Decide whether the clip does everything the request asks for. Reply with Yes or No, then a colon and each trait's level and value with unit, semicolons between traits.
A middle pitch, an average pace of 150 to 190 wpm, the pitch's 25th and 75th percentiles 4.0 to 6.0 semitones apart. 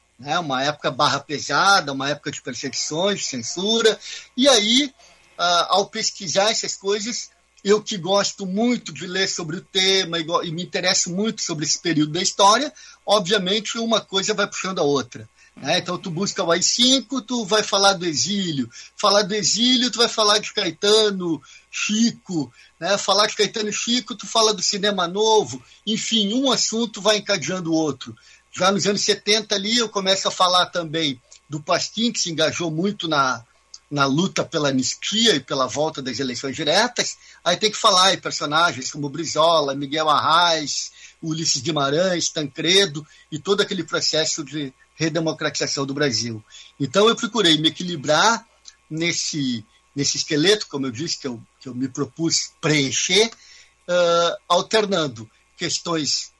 Yes: medium, 180 Hz; average, 155 wpm; average, 5.3 semitones